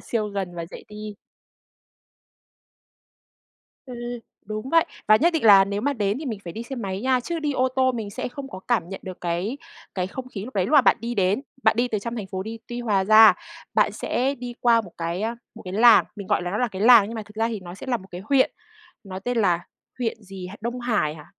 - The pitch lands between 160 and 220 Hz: Yes, high, 215 Hz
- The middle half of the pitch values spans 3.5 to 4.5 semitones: Yes, average, 4.0 semitones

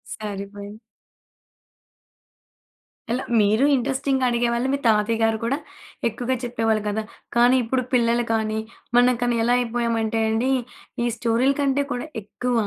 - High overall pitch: Yes, high, 235 Hz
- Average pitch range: No, narrow, 2.2 semitones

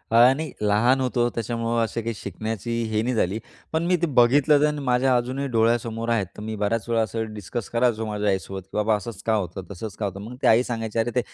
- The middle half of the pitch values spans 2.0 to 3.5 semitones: Yes, narrow, 2.4 semitones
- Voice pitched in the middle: No, low, 115 Hz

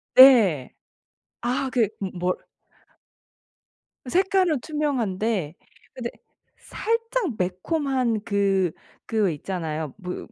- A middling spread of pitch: No, wide, 6.9 semitones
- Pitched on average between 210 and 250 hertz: Yes, high, 225 Hz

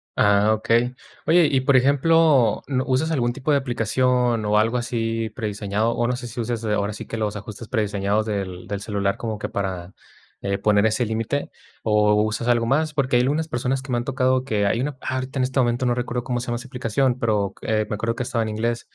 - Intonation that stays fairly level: No, average, 3.2 semitones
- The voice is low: Yes, low, 120 Hz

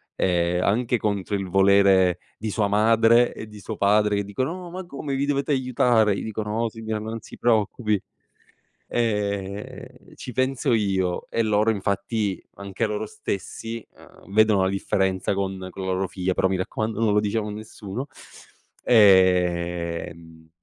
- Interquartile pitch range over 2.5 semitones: Yes, average, 2.9 semitones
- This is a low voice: Yes, low, 105 Hz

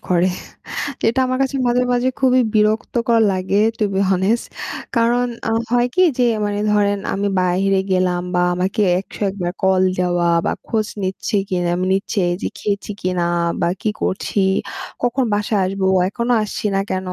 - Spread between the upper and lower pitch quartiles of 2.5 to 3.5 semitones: No, average, 4.0 semitones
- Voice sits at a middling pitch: No, high, 205 Hz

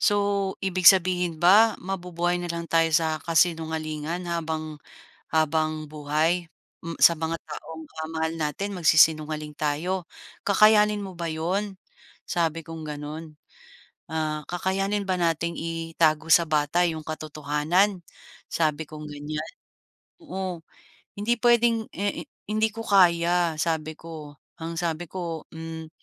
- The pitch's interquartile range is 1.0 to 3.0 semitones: Yes, narrow, 2.6 semitones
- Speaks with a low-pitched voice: No, medium, 165 Hz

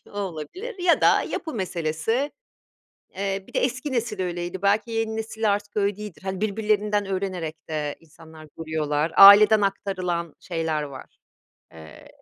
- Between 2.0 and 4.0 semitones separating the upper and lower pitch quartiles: No, average, 4.8 semitones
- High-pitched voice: Yes, high, 195 Hz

